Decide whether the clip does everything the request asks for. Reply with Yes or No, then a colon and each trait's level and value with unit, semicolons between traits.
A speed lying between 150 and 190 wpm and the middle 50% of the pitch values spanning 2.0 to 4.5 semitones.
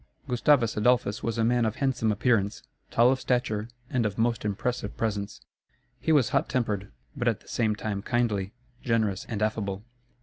Yes: average, 170 wpm; average, 2.8 semitones